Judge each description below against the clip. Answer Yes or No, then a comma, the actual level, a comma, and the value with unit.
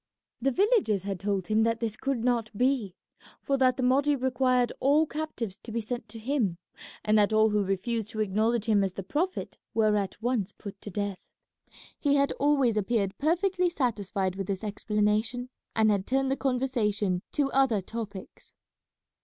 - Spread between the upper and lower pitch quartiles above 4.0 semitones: Yes, average, 4.4 semitones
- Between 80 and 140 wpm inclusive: No, average, 175 wpm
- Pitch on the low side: No, high, 225 Hz